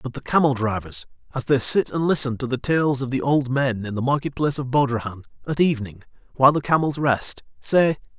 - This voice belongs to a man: Yes, male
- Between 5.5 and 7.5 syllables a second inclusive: Yes, 5.8 syllables/s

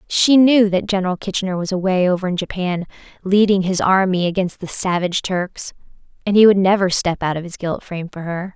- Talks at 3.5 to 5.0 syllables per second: No, 5.8 syllables/s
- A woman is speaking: Yes, female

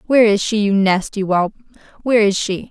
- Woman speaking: Yes, female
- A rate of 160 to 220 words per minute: Yes, average, 200 wpm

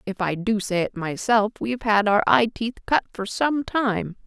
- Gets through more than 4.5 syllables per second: No, 4.4 syllables/s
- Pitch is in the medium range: No, high, 215 Hz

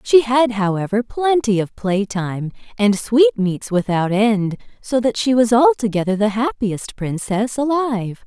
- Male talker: No, female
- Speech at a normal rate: Yes, average, 145 wpm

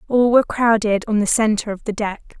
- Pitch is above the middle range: Yes, high, 220 Hz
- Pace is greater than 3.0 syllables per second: Yes, 5.9 syllables/s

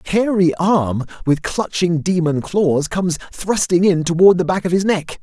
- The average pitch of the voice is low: No, medium, 175 Hz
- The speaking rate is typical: Yes, average, 185 wpm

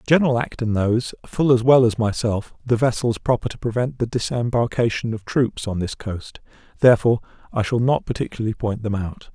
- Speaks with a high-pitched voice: No, low, 115 Hz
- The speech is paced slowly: No, average, 180 wpm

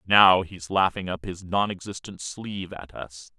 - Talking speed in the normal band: Yes, average, 160 wpm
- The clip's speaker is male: Yes, male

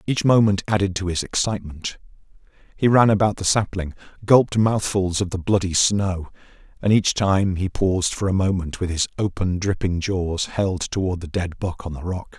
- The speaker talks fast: No, average, 185 wpm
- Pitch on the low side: Yes, very low, 95 Hz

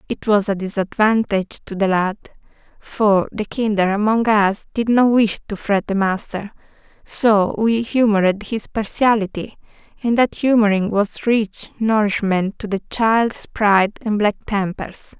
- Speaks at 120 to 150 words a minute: Yes, average, 145 wpm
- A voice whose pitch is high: Yes, high, 210 Hz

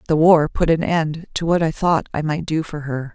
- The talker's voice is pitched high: No, medium, 160 Hz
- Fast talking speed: Yes, fast, 265 wpm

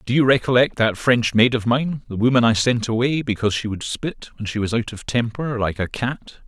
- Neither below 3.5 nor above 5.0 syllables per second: No, 5.3 syllables/s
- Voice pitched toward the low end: Yes, low, 120 Hz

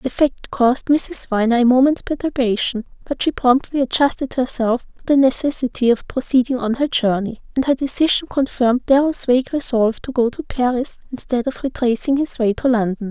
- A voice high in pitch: Yes, very high, 255 Hz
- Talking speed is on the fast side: No, average, 180 wpm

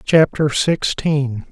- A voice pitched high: No, medium, 145 Hz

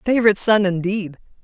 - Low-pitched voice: No, high, 200 Hz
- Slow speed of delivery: Yes, slow, 125 wpm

